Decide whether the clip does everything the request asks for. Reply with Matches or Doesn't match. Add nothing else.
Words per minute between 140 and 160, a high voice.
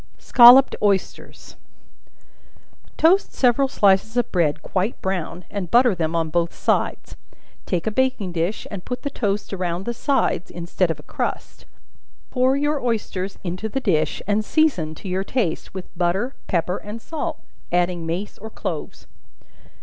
Matches